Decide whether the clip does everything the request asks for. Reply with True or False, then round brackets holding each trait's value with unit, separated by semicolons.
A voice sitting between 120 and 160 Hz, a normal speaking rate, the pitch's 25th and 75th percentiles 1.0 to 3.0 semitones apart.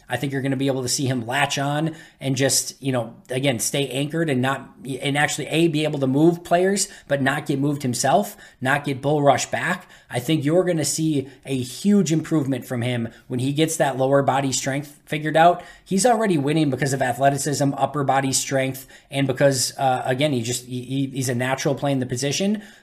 False (140 Hz; 220 wpm; 2.5 semitones)